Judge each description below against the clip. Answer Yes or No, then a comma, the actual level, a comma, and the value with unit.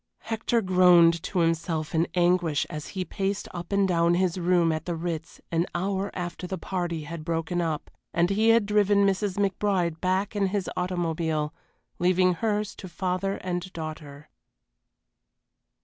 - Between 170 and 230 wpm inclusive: No, average, 155 wpm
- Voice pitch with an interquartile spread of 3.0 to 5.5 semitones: No, narrow, 2.6 semitones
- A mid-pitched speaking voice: Yes, medium, 180 Hz